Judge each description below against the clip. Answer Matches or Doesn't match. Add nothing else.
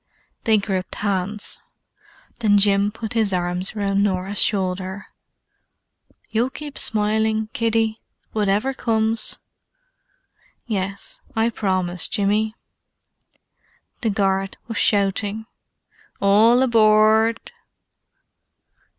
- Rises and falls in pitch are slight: Matches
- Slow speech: Matches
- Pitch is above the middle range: Matches